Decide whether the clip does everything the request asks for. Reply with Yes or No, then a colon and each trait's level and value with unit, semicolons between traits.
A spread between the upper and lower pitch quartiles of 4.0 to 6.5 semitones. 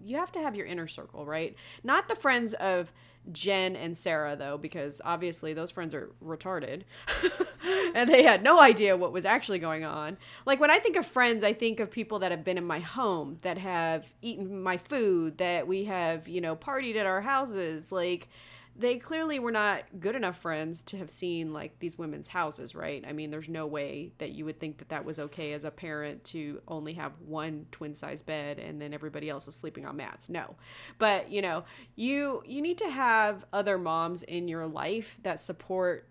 Yes: average, 5.1 semitones